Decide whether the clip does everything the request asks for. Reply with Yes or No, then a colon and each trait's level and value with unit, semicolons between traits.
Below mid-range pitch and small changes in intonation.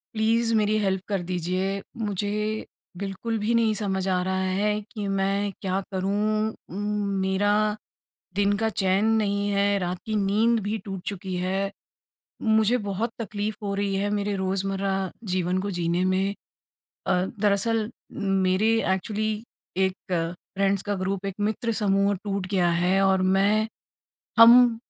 No: high, 200 Hz; narrow, 1.9 semitones